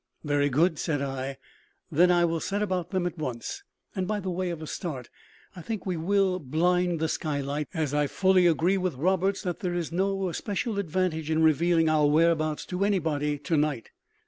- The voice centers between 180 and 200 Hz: No, medium, 170 Hz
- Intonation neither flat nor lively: Yes, average, 3.6 semitones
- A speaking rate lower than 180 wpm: No, average, 190 wpm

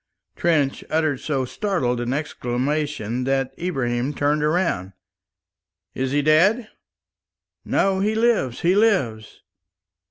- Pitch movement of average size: No, wide, 5.9 semitones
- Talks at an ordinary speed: No, slow, 105 wpm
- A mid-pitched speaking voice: Yes, medium, 145 Hz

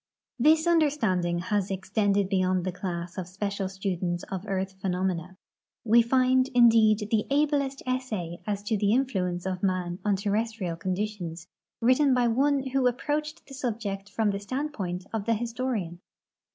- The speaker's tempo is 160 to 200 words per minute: No, average, 150 wpm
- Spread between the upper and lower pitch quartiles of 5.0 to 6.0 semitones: Yes, average, 5.3 semitones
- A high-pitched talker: Yes, high, 205 Hz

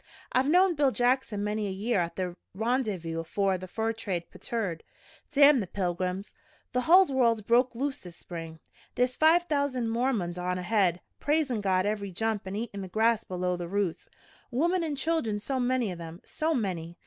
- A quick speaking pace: No, average, 180 wpm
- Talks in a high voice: Yes, high, 215 Hz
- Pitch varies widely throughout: Yes, wide, 5.9 semitones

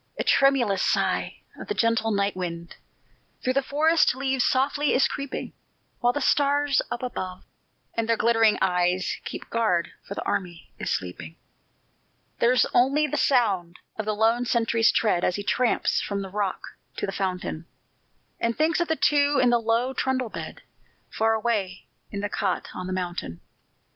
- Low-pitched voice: No, high, 225 Hz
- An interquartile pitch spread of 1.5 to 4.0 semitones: No, wide, 5.5 semitones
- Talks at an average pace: Yes, average, 170 wpm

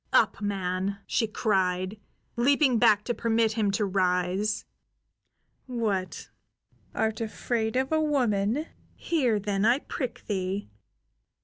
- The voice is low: No, high, 215 Hz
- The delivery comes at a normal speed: No, slow, 115 wpm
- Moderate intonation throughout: Yes, average, 3.5 semitones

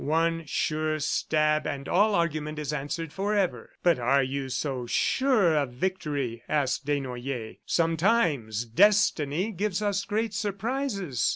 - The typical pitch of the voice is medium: Yes, medium, 155 Hz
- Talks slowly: Yes, slow, 125 wpm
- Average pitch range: No, wide, 6.1 semitones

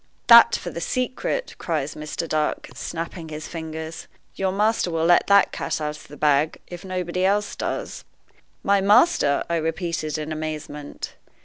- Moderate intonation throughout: Yes, average, 3.7 semitones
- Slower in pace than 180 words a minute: Yes, average, 155 wpm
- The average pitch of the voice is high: No, medium, 165 Hz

